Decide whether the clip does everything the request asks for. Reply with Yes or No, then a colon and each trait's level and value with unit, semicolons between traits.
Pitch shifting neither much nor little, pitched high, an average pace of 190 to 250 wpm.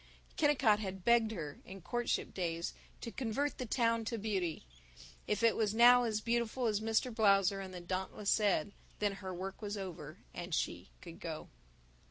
No: average, 3.7 semitones; high, 210 Hz; average, 175 wpm